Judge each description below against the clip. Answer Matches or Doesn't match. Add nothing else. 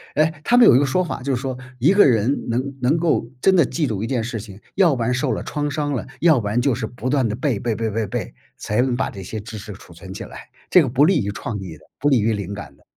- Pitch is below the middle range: Matches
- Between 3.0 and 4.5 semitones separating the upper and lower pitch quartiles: Doesn't match